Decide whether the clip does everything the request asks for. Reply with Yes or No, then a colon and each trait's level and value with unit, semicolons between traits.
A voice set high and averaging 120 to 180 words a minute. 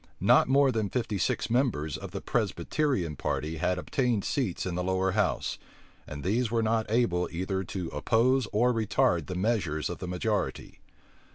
No: low, 100 Hz; average, 175 wpm